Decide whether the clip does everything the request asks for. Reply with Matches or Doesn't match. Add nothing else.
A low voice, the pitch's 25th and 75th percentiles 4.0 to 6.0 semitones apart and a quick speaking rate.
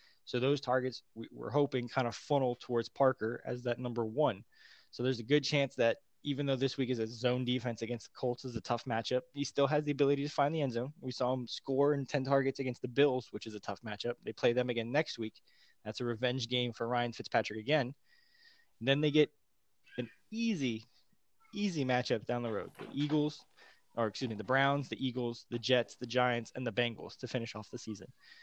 Doesn't match